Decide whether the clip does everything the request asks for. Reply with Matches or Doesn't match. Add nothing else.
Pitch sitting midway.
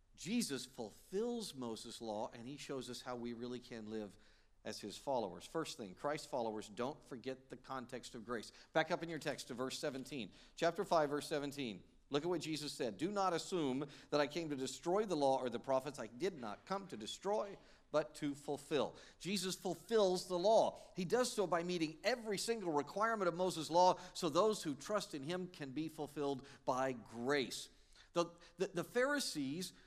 Matches